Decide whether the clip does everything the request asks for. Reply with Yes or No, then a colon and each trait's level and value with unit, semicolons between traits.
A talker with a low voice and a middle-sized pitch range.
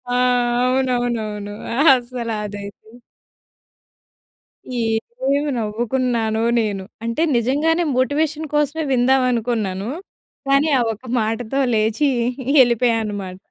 No: high, 240 Hz; average, 3.4 semitones